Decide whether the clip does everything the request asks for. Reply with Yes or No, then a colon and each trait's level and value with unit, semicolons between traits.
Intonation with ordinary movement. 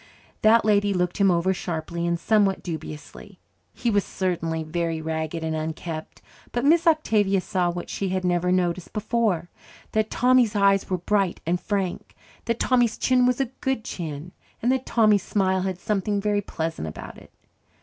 Yes: average, 4.1 semitones